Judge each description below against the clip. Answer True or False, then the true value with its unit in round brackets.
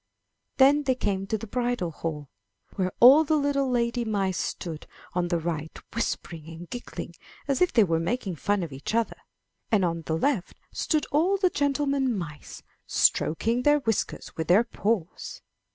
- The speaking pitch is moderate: False (220 Hz)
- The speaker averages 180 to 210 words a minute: False (170 wpm)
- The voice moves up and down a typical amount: False (7.5 semitones)